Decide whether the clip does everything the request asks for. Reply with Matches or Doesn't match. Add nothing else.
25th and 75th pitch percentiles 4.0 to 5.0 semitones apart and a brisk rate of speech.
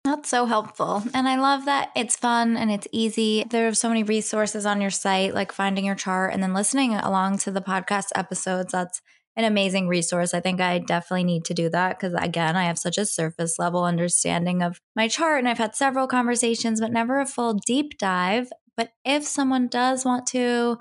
Matches